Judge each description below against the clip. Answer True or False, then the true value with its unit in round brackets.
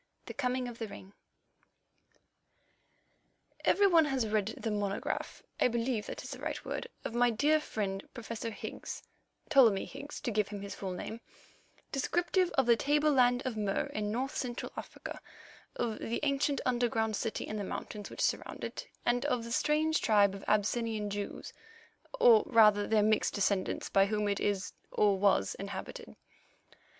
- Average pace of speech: True (160 wpm)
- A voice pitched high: True (225 Hz)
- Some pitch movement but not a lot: True (4.0 semitones)